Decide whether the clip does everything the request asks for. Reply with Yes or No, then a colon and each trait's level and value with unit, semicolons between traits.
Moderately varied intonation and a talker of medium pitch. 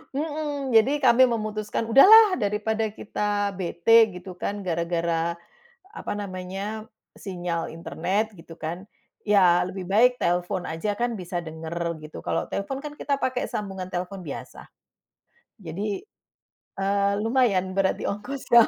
No: average, 4.3 semitones; high, 200 Hz